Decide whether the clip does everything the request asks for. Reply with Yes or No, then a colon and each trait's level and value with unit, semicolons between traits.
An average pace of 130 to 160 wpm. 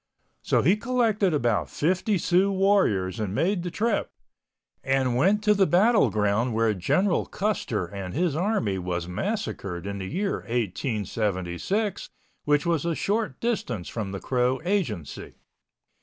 Yes: average, 140 wpm